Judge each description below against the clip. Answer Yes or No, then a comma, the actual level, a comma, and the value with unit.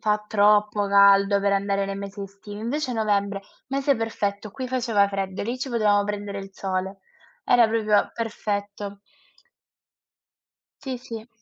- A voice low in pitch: No, high, 205 Hz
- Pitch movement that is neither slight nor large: No, narrow, 2.1 semitones